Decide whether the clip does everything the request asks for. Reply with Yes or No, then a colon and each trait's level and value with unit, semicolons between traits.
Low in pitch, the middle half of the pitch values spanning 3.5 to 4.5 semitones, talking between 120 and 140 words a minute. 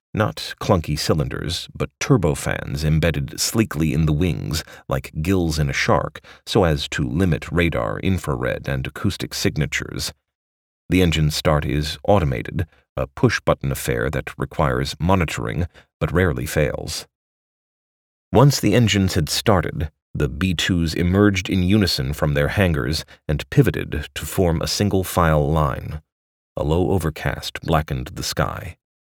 Yes: very low, 80 Hz; average, 4.2 semitones; slow, 135 wpm